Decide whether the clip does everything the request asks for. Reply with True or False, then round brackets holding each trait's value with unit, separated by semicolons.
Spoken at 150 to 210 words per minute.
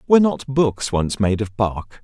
True (205 wpm)